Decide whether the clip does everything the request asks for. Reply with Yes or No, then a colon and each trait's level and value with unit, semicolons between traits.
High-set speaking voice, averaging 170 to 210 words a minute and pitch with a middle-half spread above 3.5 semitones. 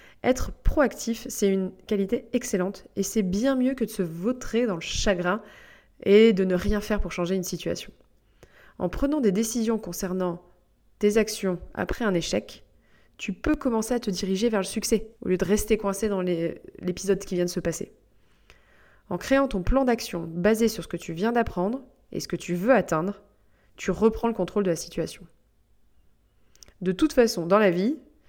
Yes: high, 200 Hz; average, 190 wpm; average, 4.1 semitones